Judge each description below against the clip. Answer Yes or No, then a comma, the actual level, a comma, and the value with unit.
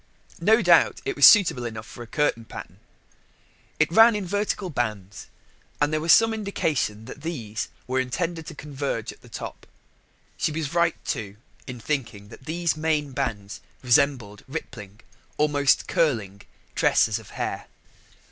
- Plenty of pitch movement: Yes, wide, 6.5 semitones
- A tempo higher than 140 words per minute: Yes, average, 150 wpm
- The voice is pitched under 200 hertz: Yes, medium, 140 Hz